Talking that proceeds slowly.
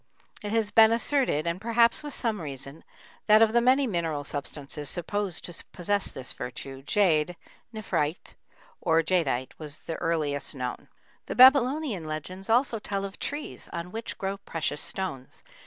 No: average, 155 wpm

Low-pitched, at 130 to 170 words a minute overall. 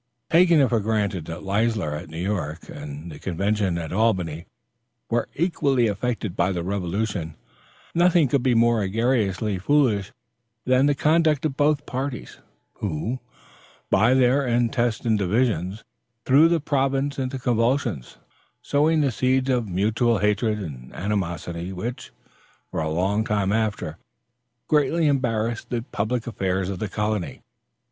Yes: low, 110 Hz; average, 140 wpm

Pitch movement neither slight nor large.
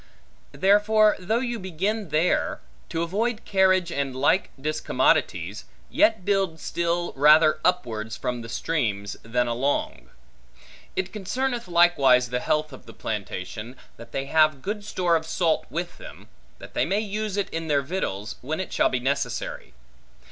No: wide, 6.7 semitones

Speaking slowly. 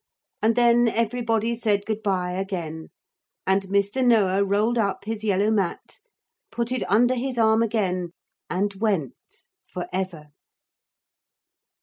Yes: slow, 125 wpm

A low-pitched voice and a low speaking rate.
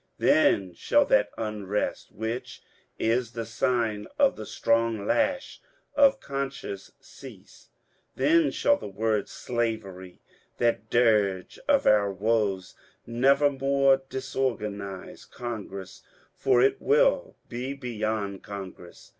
Yes: low, 115 Hz; slow, 120 wpm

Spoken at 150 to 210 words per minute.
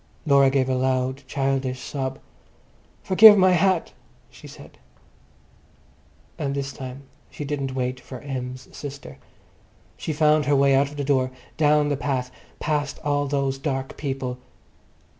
No: average, 140 wpm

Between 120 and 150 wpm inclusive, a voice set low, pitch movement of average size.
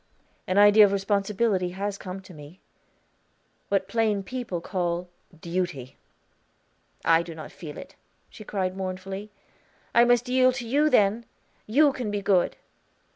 No: average, 140 wpm; high, 195 Hz; average, 3.6 semitones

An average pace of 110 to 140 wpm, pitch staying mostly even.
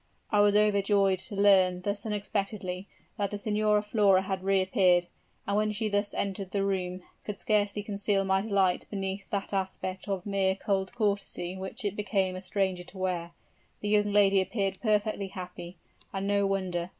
No: average, 165 wpm; narrow, 1.5 semitones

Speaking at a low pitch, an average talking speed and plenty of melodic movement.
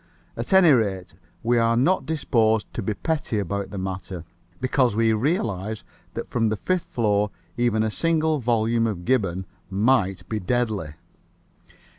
No: low, 110 Hz; average, 150 wpm; average, 3.9 semitones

